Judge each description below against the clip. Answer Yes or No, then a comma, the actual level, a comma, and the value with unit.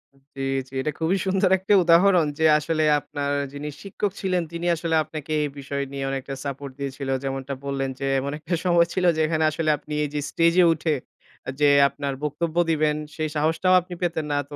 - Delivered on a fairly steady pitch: No, average, 3.2 semitones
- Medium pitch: Yes, medium, 155 Hz